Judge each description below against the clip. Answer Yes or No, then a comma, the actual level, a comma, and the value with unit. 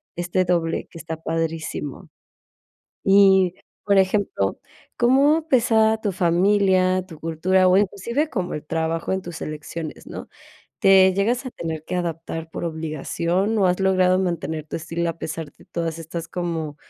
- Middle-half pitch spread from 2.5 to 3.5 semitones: Yes, average, 3.0 semitones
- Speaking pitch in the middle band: Yes, medium, 180 Hz